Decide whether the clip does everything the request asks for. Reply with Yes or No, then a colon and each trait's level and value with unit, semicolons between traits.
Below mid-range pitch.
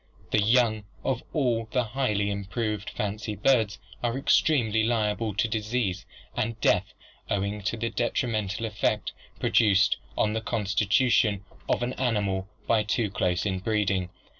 Yes: low, 110 Hz